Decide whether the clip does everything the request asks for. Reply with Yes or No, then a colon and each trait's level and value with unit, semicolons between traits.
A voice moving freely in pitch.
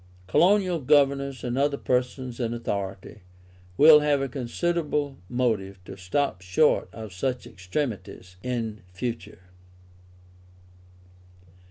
Yes: wide, 5.7 semitones